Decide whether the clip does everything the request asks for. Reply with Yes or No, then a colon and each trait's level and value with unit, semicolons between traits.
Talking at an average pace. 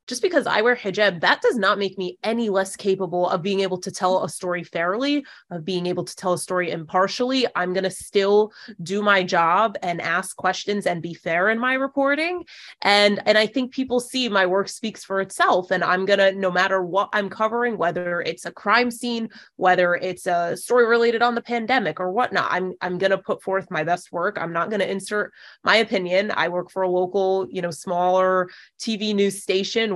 No: fast, 205 wpm